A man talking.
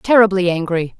No: female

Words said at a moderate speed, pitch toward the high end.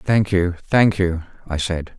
No: average, 180 wpm; very low, 90 Hz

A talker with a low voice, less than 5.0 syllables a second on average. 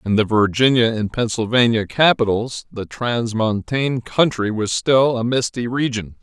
Yes: low, 115 Hz; 4.5 syllables/s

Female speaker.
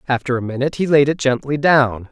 No: male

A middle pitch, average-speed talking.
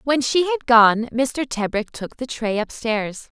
No: high, 240 Hz; average, 175 wpm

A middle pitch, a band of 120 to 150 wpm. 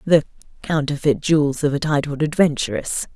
Yes: medium, 150 Hz; slow, 135 wpm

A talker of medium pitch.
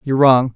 No: low, 130 Hz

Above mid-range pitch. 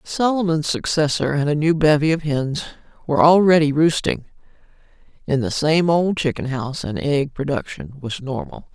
No: medium, 150 Hz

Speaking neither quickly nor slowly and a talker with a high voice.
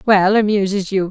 Yes: average, 165 wpm; high, 195 Hz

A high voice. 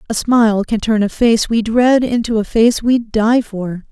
Yes: high, 225 Hz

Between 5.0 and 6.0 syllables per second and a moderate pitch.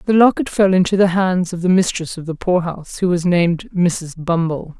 Yes: 5.3 syllables/s; medium, 180 Hz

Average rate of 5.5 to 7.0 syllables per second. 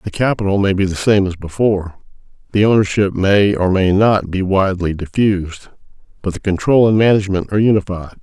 Yes: 5.8 syllables/s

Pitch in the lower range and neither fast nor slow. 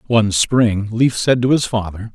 Yes: low, 115 Hz; average, 195 wpm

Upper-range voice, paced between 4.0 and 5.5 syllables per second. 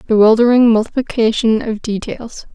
Yes: high, 225 Hz; 5.1 syllables/s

